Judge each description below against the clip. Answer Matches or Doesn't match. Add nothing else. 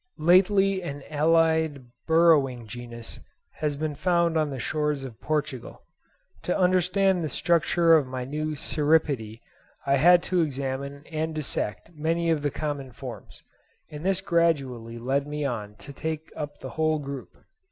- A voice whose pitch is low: Doesn't match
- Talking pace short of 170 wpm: Matches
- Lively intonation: Doesn't match